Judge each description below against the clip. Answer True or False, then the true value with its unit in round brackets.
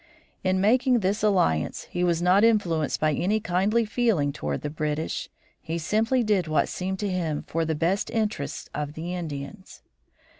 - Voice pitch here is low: False (180 Hz)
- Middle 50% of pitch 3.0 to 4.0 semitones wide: False (5.2 semitones)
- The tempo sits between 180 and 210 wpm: False (165 wpm)